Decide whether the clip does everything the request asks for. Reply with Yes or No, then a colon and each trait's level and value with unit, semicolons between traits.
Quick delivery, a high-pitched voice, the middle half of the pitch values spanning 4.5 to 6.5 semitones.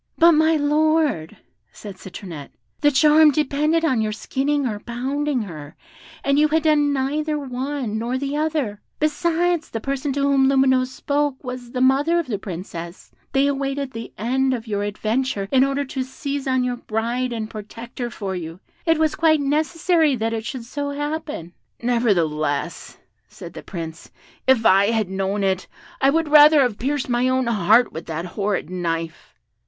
No: average, 170 wpm; very high, 260 Hz; wide, 5.5 semitones